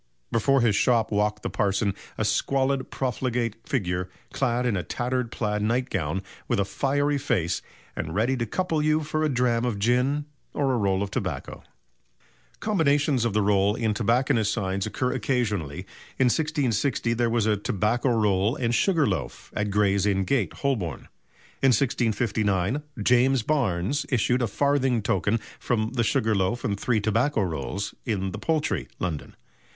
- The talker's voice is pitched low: Yes, low, 115 Hz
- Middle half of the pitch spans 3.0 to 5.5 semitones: Yes, average, 4.6 semitones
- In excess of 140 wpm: Yes, average, 155 wpm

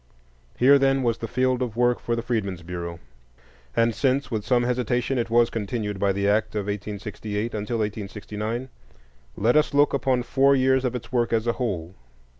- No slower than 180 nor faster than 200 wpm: Yes, average, 185 wpm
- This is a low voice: Yes, low, 115 Hz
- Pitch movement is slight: No, average, 3.4 semitones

